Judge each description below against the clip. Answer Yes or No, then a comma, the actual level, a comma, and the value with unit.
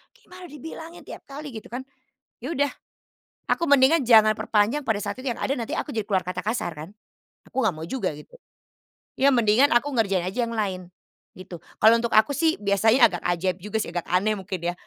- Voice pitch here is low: No, high, 220 Hz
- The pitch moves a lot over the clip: Yes, wide, 6.1 semitones